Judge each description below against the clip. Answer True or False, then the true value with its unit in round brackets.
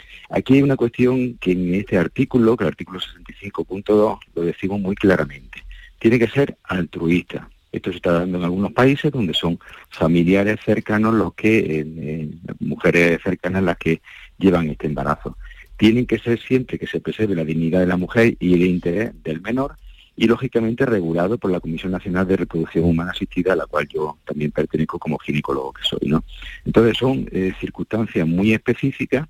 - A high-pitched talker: False (95 Hz)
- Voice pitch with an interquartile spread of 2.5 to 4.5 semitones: False (5.1 semitones)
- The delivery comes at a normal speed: True (180 wpm)